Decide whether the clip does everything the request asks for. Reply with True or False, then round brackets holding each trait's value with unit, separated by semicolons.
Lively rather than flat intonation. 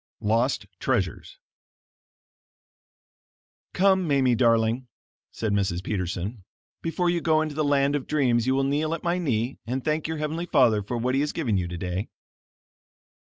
True (5.7 semitones)